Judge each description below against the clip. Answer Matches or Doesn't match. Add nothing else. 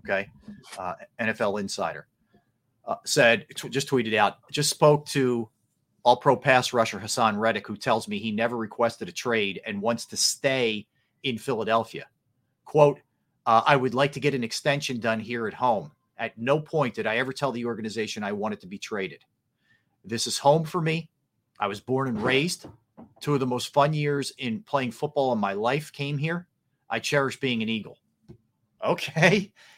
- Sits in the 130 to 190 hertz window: Matches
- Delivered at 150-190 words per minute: Matches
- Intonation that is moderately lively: Matches